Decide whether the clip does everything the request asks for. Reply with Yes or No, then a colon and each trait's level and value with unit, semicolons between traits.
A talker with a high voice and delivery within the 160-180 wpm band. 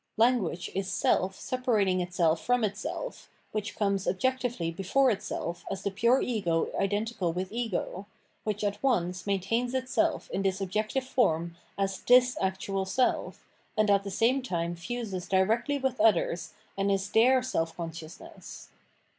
No: high, 200 Hz; average, 145 wpm